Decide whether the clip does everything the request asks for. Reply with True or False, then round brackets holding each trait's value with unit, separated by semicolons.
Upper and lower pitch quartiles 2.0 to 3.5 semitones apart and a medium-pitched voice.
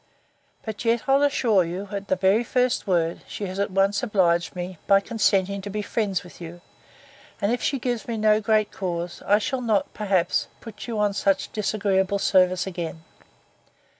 False (2.8 semitones; 200 Hz)